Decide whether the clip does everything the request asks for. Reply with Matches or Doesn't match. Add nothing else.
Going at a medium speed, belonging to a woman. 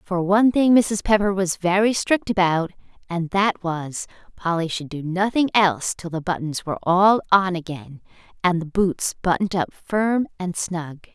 Matches